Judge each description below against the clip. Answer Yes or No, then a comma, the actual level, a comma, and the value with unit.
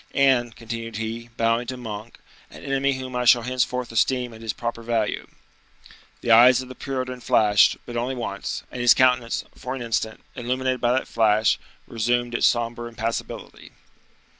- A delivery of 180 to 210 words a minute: No, average, 165 wpm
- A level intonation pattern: Yes, narrow, 1.8 semitones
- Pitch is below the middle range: Yes, low, 120 Hz